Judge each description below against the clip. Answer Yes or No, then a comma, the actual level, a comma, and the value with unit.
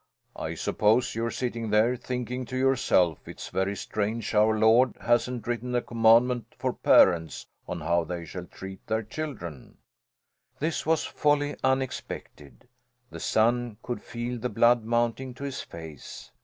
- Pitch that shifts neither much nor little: Yes, average, 3.0 semitones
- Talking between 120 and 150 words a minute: Yes, average, 145 wpm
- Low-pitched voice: Yes, low, 115 Hz